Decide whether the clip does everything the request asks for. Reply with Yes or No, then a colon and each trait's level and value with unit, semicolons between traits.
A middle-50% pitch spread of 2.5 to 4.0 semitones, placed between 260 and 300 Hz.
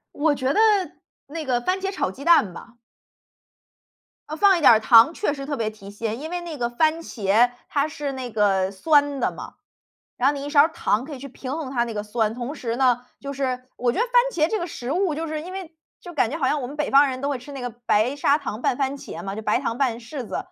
No: average, 4.4 semitones; very high, 275 Hz